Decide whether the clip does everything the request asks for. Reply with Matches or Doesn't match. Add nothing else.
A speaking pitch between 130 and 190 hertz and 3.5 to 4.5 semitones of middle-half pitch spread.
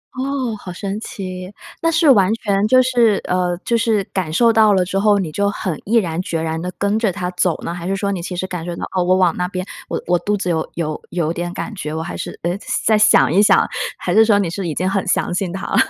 Doesn't match